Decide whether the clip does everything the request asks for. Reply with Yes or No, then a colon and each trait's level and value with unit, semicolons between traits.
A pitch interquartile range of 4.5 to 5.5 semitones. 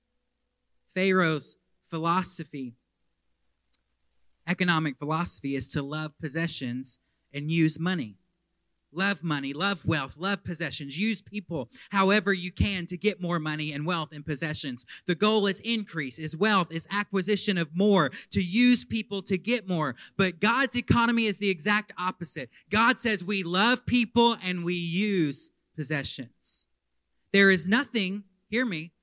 Yes: average, 5.1 semitones